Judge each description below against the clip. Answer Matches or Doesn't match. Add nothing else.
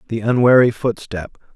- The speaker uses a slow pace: Matches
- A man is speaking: Matches